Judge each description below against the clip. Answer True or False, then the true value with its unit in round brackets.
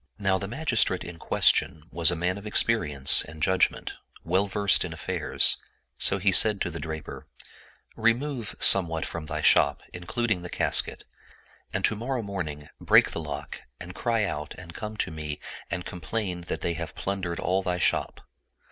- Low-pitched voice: True (90 Hz)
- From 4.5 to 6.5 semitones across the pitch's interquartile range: False (4.1 semitones)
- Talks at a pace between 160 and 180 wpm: True (175 wpm)